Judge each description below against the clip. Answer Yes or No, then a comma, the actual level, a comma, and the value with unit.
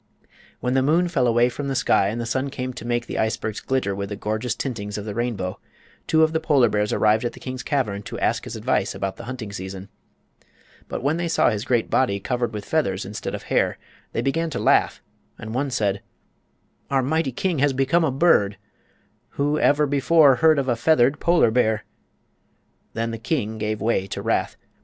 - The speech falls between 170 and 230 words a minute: Yes, fast, 205 wpm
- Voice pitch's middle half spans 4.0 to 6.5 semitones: Yes, average, 4.7 semitones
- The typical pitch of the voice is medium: No, low, 125 Hz